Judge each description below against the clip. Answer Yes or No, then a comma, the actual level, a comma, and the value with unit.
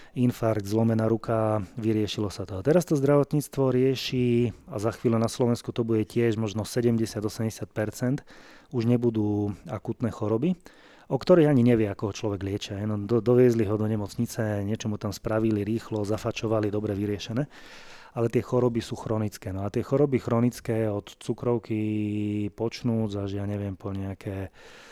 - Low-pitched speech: Yes, low, 110 Hz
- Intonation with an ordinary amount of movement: No, narrow, 2.3 semitones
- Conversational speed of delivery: Yes, average, 155 wpm